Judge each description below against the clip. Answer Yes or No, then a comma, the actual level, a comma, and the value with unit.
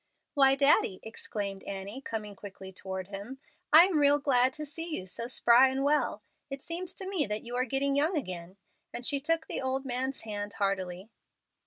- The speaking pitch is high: Yes, very high, 255 Hz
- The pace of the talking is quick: No, average, 190 wpm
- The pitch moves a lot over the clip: Yes, wide, 6.0 semitones